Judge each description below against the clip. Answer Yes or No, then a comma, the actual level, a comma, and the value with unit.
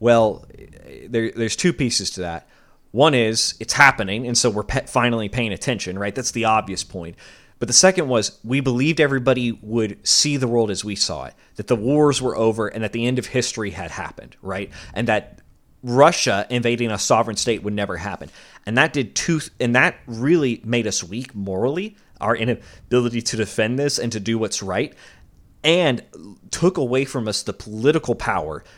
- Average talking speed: Yes, average, 185 wpm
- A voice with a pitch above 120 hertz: No, low, 115 Hz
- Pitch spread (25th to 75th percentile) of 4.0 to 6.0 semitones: No, average, 3.4 semitones